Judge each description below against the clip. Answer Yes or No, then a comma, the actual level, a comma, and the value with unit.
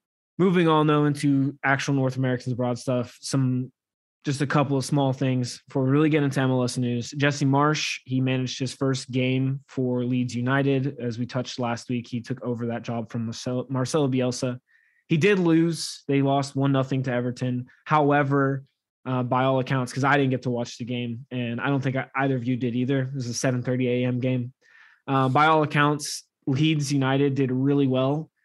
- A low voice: Yes, low, 130 Hz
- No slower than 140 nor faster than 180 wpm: No, average, 190 wpm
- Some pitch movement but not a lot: No, narrow, 2.0 semitones